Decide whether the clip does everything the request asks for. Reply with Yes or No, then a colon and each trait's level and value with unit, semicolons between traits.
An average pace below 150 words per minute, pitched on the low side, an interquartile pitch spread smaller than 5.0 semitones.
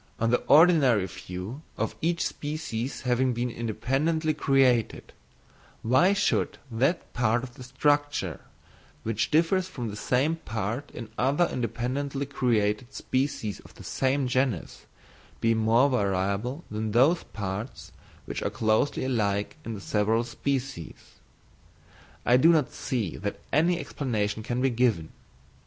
Yes: slow, 135 wpm; low, 125 Hz; average, 4.3 semitones